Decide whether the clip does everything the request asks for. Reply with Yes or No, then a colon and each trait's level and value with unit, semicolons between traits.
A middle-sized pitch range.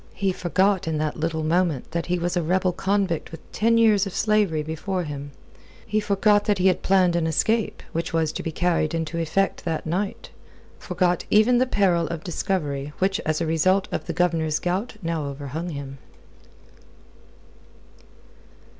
Yes: average, 3.4 semitones